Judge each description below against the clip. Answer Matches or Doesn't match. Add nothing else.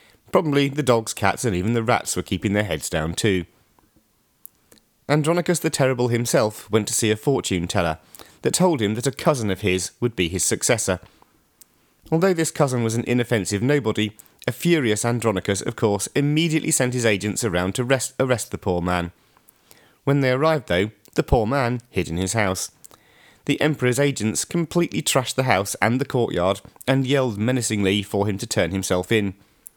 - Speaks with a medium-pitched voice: Doesn't match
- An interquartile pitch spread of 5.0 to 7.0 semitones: Matches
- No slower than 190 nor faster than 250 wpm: Doesn't match